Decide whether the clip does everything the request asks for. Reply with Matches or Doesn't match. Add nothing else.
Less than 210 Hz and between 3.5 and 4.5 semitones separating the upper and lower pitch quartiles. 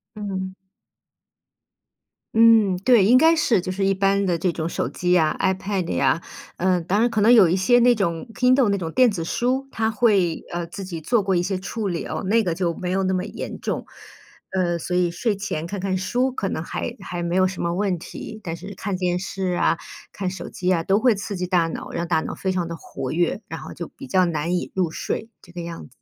Doesn't match